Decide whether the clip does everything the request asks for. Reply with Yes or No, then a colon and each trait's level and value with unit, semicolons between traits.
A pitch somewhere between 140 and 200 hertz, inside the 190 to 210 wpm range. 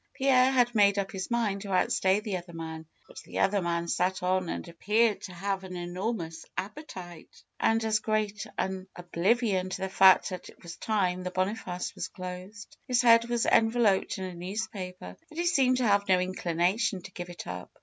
Yes: high, 190 Hz; average, 200 wpm